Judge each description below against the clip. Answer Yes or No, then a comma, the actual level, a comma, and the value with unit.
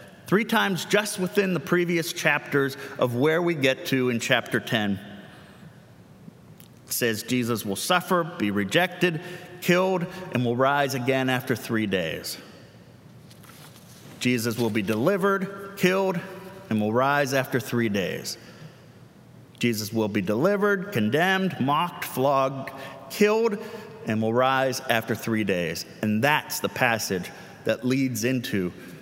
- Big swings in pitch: Yes, wide, 7.3 semitones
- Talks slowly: Yes, slow, 130 wpm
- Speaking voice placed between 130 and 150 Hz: Yes, low, 135 Hz